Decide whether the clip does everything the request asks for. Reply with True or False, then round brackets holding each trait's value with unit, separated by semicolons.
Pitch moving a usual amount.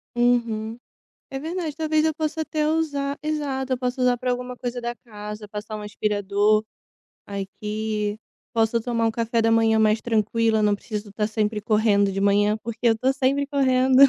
True (3.8 semitones)